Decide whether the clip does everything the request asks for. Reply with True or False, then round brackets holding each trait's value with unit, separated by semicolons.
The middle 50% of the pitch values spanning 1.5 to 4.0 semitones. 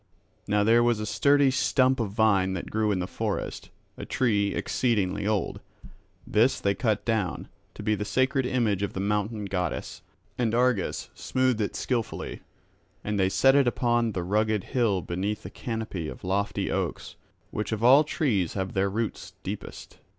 True (3.2 semitones)